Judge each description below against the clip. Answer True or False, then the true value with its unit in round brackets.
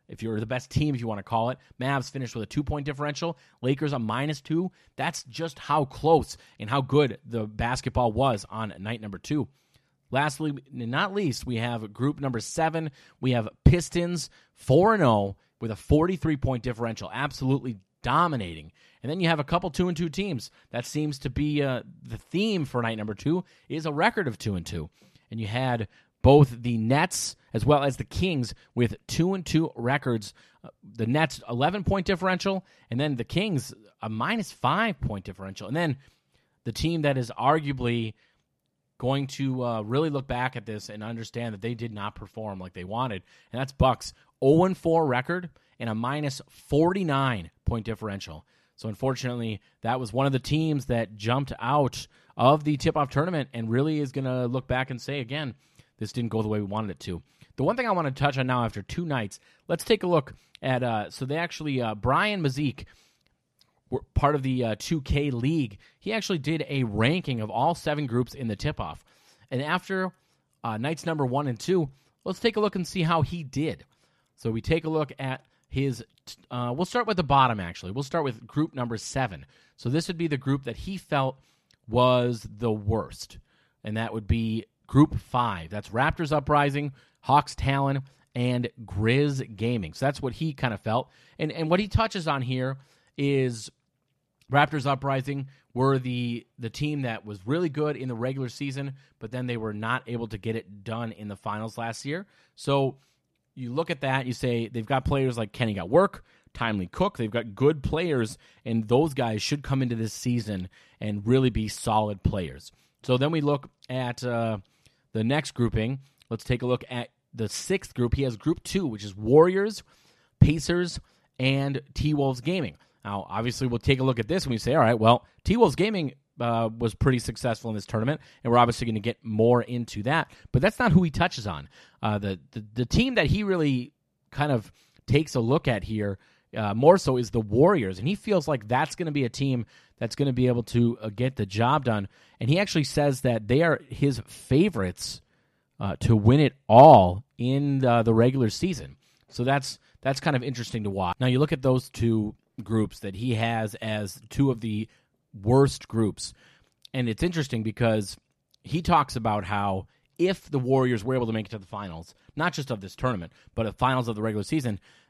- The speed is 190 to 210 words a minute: True (200 wpm)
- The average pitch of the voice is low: True (130 Hz)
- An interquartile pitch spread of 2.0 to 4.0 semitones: False (4.5 semitones)